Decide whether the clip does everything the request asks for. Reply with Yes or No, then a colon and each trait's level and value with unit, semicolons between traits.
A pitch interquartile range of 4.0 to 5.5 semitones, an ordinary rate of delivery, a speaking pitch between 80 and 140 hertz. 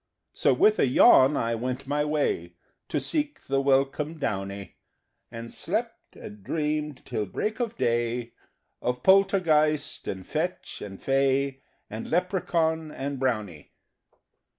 No: average, 5.1 semitones; slow, 130 wpm; low, 135 Hz